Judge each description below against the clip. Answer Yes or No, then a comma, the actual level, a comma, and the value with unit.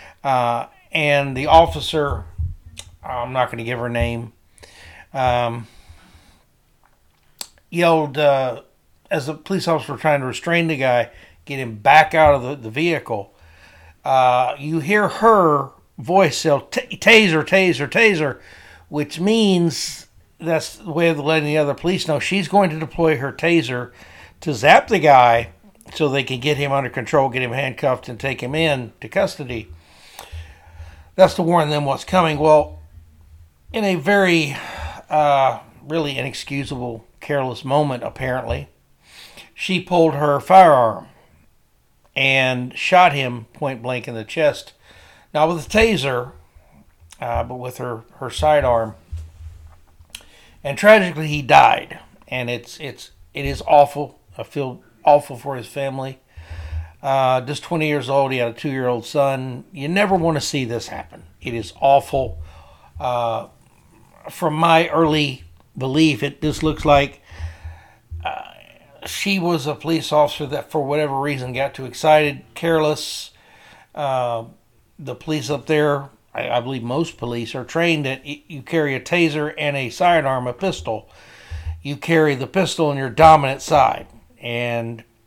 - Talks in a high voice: No, medium, 140 Hz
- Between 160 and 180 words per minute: No, average, 145 wpm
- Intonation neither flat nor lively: Yes, average, 4.9 semitones